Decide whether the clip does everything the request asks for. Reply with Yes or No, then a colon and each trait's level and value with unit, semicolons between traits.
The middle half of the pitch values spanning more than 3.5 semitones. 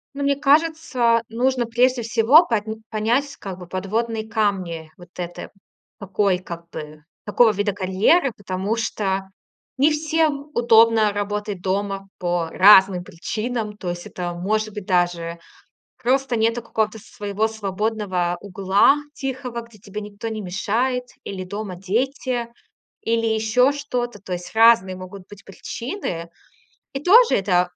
Yes: average, 4.2 semitones